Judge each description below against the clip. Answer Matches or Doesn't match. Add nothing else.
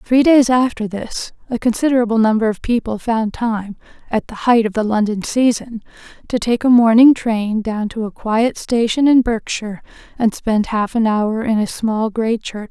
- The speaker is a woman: Matches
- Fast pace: Matches